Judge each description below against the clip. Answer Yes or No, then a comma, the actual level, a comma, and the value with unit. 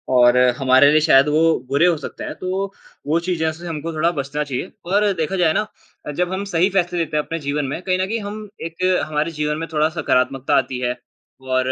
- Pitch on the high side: No, medium, 155 Hz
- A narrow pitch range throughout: No, average, 3.8 semitones